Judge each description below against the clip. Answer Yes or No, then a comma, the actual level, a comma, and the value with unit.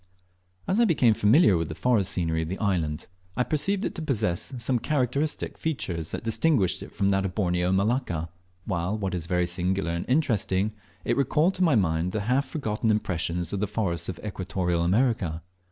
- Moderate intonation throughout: No, wide, 6.1 semitones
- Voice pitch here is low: Yes, low, 100 Hz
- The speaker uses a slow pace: No, average, 190 wpm